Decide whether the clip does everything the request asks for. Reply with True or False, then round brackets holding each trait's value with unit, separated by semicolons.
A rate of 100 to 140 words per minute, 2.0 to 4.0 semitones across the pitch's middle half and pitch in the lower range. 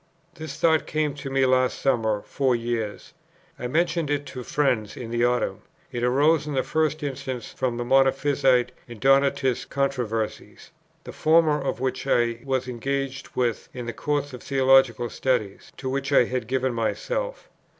False (170 wpm; 2.7 semitones; 130 Hz)